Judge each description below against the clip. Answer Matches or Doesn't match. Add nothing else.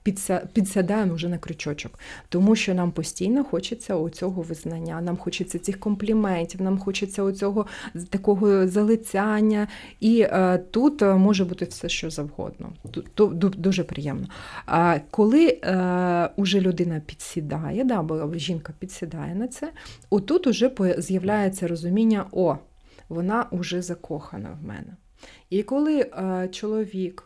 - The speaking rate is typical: Matches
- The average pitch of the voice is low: Doesn't match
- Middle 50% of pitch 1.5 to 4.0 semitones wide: Matches